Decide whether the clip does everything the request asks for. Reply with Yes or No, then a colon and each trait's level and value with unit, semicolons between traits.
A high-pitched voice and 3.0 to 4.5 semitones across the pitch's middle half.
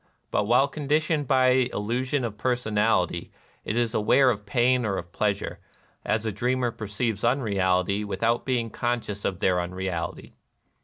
No: low, 115 Hz; average, 3.9 semitones